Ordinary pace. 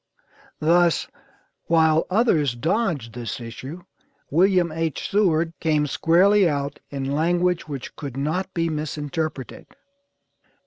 No: slow, 105 wpm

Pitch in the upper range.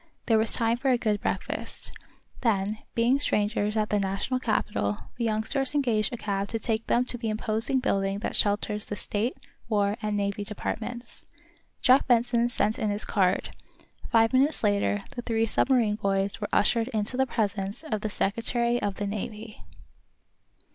Yes: high, 220 Hz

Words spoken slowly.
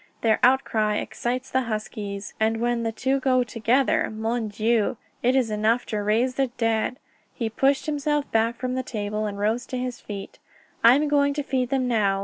No: average, 190 wpm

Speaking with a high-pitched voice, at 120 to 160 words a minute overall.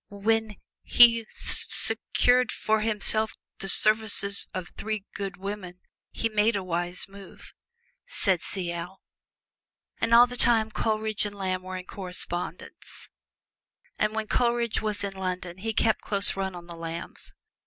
Yes: high, 200 Hz; average, 145 wpm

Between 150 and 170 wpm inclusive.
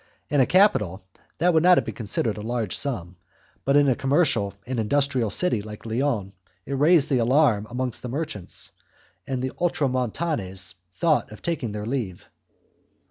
Yes: average, 165 wpm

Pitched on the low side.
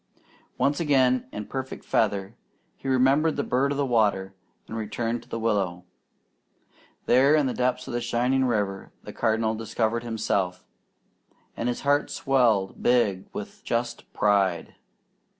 Yes: low, 120 Hz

